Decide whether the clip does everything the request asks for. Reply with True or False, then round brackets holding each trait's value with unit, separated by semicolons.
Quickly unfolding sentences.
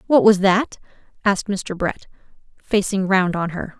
False (160 wpm)